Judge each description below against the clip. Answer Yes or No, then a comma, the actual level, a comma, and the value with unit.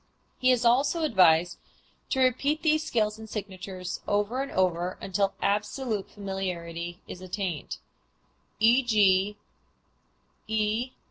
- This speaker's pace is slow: Yes, slow, 105 wpm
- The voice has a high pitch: Yes, high, 205 Hz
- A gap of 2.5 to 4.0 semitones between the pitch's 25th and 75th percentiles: No, average, 4.7 semitones